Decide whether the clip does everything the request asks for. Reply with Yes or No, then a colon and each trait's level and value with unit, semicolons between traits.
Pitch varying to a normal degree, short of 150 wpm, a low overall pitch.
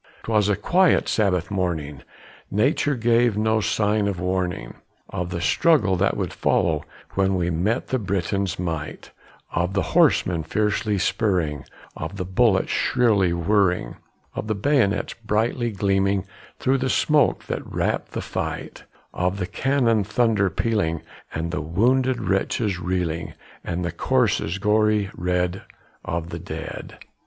Yes: average, 3.7 semitones; average, 140 wpm; low, 100 Hz